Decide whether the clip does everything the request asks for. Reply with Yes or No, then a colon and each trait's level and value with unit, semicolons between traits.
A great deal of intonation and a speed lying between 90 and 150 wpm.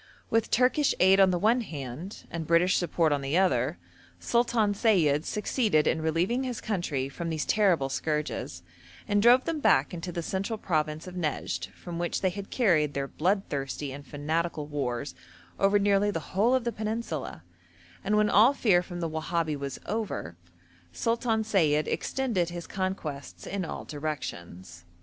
No: wide, 5.7 semitones; average, 165 wpm